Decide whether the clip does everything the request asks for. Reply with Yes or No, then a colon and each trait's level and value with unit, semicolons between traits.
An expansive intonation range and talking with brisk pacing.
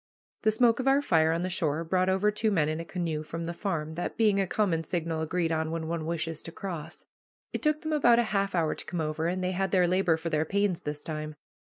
No: average, 3.6 semitones; fast, 255 wpm